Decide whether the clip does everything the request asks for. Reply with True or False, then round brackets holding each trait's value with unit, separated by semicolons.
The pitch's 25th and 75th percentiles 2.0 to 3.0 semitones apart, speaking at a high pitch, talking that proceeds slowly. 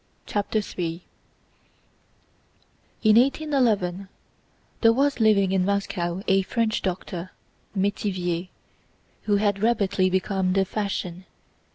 True (2.7 semitones; 195 Hz; 85 wpm)